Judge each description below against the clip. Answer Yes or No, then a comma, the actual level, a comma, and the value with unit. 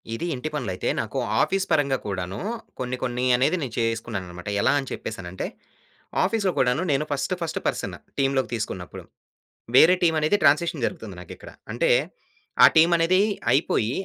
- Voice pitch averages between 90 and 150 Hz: Yes, low, 135 Hz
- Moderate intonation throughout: No, wide, 6.3 semitones